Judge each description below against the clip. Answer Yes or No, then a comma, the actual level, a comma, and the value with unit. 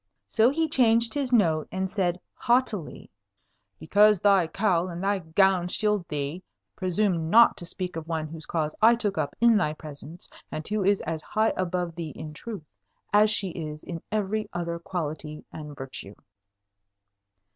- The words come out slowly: No, average, 165 wpm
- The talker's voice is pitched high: No, medium, 180 Hz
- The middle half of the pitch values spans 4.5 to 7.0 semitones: Yes, average, 4.8 semitones